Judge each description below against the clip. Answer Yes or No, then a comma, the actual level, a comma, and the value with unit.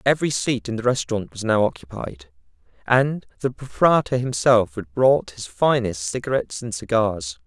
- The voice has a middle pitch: No, low, 115 Hz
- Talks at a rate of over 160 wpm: No, average, 155 wpm